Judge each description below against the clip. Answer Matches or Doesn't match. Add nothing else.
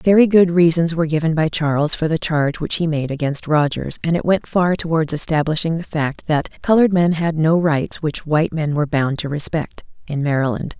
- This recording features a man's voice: Doesn't match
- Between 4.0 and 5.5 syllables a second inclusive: Matches